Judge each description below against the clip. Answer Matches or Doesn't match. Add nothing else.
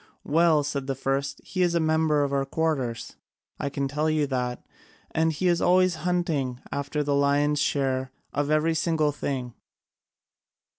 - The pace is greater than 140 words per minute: Matches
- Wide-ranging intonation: Doesn't match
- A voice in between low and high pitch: Matches